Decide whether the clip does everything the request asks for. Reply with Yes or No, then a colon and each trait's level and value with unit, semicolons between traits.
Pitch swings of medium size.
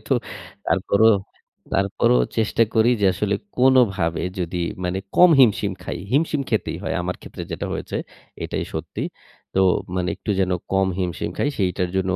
Yes: average, 3.5 semitones